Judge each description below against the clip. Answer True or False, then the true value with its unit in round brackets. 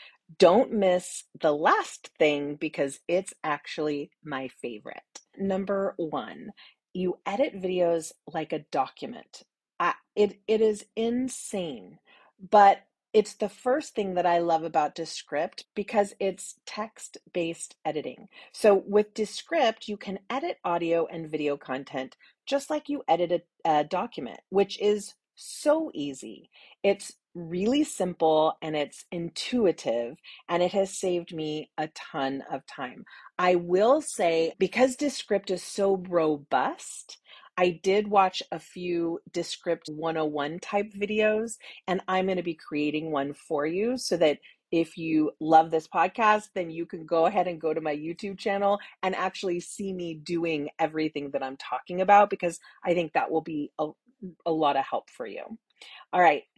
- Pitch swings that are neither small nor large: True (4.3 semitones)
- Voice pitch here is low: False (180 Hz)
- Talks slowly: False (150 wpm)